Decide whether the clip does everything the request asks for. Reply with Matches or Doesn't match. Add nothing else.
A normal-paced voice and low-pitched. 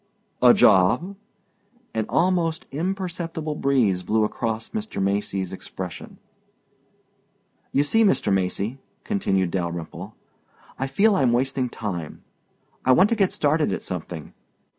Doesn't match